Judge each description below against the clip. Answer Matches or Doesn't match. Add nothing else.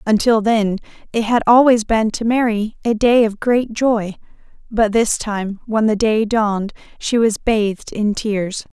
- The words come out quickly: Doesn't match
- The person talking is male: Doesn't match